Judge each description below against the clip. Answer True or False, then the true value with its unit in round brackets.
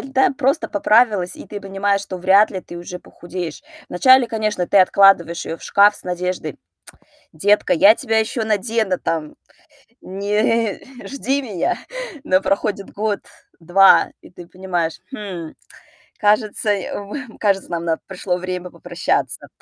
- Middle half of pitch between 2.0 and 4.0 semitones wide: True (3.1 semitones)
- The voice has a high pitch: True (195 Hz)